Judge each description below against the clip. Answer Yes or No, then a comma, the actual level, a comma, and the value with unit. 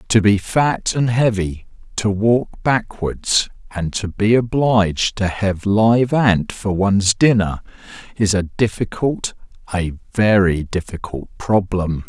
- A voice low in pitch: Yes, low, 105 Hz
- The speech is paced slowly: Yes, slow, 130 wpm